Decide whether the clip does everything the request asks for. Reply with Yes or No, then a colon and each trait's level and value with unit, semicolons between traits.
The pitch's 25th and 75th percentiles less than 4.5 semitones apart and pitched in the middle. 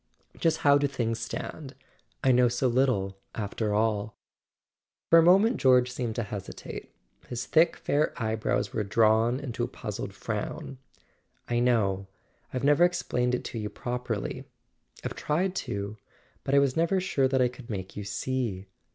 No: average, 4.1 semitones; low, 125 Hz